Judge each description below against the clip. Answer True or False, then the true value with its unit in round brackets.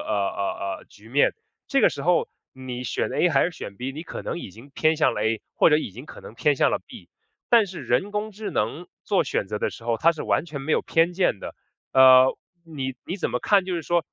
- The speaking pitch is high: False (145 Hz)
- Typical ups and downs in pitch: False (6.5 semitones)